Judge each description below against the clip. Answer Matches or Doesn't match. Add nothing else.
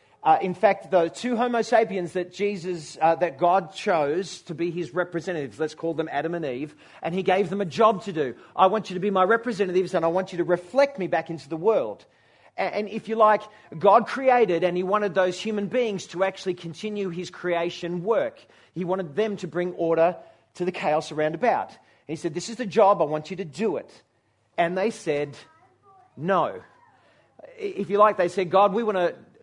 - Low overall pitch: Doesn't match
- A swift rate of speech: Matches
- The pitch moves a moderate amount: Matches